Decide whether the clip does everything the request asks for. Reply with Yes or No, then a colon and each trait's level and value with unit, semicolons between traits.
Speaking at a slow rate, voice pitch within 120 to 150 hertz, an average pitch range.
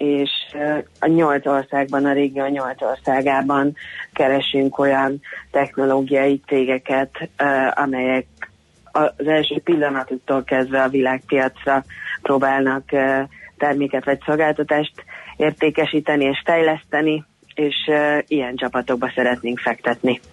No: slow, 95 wpm; medium, 140 Hz; narrow, 1.8 semitones